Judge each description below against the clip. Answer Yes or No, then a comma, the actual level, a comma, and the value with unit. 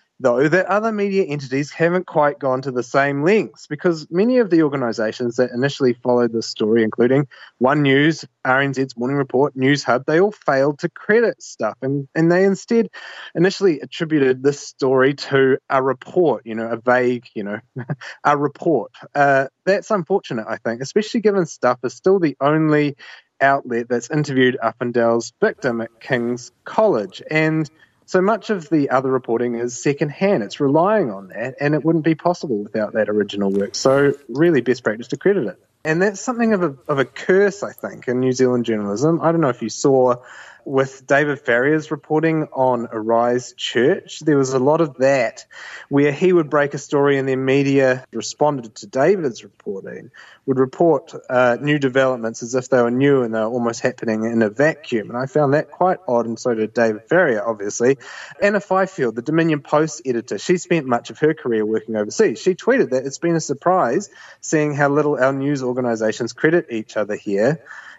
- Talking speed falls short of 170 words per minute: No, average, 185 wpm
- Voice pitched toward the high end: No, low, 135 Hz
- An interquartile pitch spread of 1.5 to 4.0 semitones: No, average, 4.4 semitones